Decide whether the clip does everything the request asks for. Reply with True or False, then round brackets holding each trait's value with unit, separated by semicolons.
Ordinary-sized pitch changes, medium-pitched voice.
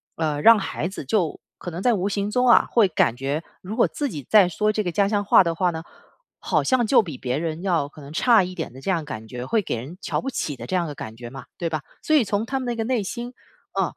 False (6.4 semitones; 180 Hz)